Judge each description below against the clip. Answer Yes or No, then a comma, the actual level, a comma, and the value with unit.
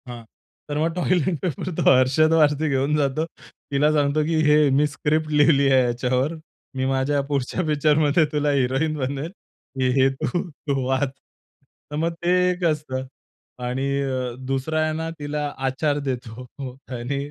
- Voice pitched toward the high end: No, medium, 145 Hz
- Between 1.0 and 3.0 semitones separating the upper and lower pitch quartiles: Yes, narrow, 2.6 semitones